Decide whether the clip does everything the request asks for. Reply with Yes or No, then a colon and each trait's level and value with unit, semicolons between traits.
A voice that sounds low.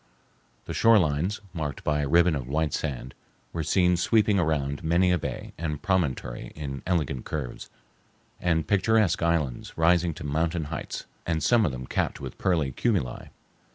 Yes: very low, 80 Hz